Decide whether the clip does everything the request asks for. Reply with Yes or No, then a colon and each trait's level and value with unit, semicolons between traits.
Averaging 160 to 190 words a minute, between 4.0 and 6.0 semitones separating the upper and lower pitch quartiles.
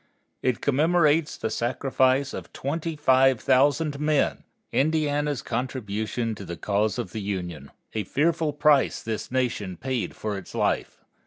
No: average, 140 wpm; average, 5.2 semitones